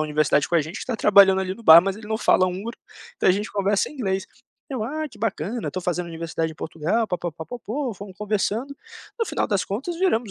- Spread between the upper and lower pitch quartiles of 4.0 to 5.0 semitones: Yes, average, 4.3 semitones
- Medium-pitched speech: No, high, 200 Hz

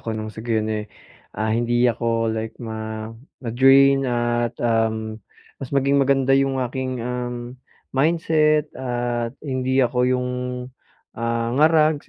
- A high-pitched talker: No, low, 120 Hz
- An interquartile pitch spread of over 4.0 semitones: No, average, 2.8 semitones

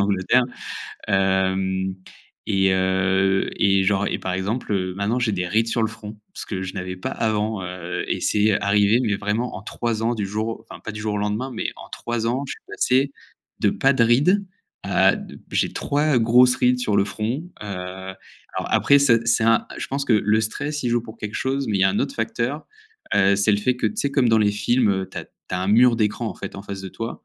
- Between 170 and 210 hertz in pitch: No, low, 105 Hz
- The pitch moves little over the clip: No, average, 3.7 semitones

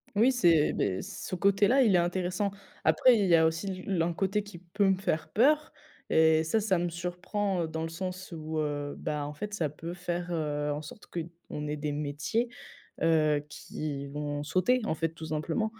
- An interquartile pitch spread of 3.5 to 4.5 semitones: Yes, average, 4.1 semitones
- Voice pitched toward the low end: No, medium, 170 Hz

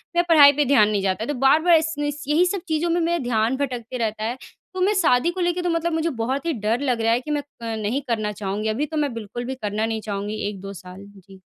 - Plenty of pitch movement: Yes, wide, 6.5 semitones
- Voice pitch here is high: Yes, high, 245 Hz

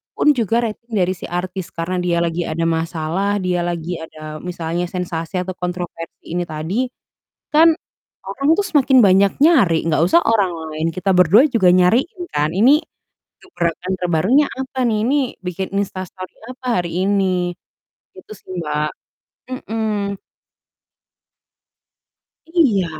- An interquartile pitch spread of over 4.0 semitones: Yes, average, 4.7 semitones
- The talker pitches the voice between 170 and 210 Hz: Yes, medium, 185 Hz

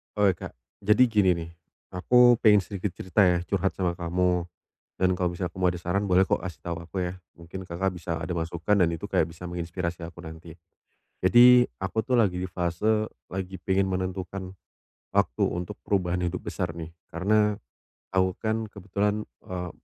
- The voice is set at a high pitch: No, very low, 90 Hz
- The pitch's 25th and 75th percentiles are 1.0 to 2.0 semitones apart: No, narrow, 2.5 semitones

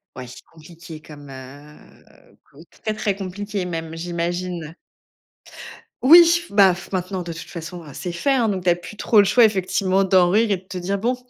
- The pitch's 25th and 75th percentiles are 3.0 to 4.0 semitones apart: Yes, average, 3.3 semitones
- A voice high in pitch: No, medium, 180 Hz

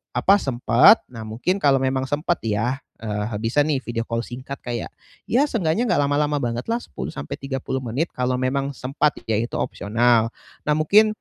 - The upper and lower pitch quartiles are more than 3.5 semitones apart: Yes, average, 4.1 semitones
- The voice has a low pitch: Yes, low, 130 Hz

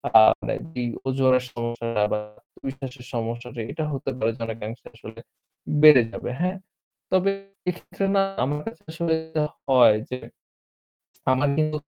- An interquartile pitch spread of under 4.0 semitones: No, average, 4.6 semitones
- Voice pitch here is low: Yes, low, 130 Hz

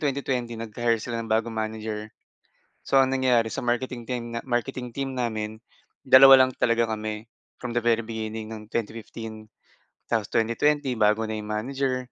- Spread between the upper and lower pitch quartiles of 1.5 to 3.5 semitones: Yes, narrow, 2.5 semitones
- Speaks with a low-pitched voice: Yes, low, 115 Hz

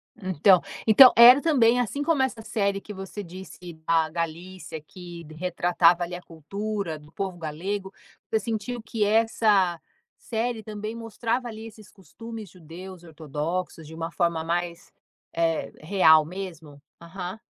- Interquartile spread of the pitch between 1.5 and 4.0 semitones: No, average, 4.6 semitones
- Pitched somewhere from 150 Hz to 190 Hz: Yes, medium, 185 Hz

